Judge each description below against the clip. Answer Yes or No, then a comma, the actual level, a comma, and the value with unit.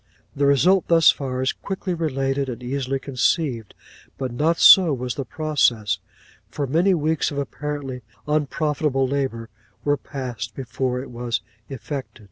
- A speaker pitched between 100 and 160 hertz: Yes, low, 135 Hz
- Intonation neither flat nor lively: Yes, average, 3.0 semitones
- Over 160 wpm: No, average, 140 wpm